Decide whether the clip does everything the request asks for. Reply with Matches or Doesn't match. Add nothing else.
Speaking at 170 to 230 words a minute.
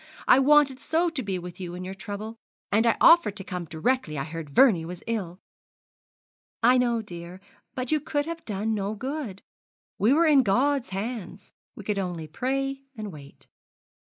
Matches